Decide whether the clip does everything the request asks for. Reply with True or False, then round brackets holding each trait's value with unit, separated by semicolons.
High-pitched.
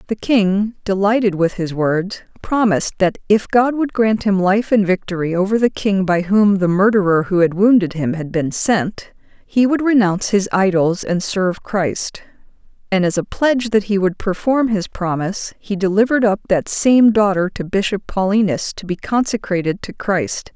True (200 Hz)